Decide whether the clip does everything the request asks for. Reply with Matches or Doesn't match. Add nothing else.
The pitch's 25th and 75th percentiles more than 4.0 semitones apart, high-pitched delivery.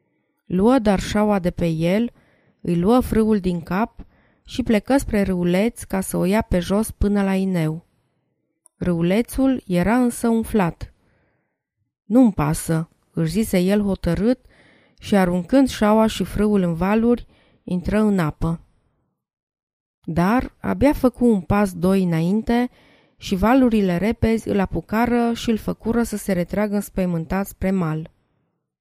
Matches